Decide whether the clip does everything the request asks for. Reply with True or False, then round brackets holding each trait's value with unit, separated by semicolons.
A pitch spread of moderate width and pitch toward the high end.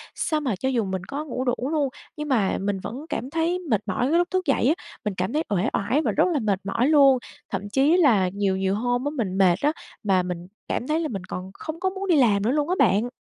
False (7.4 semitones; 250 Hz)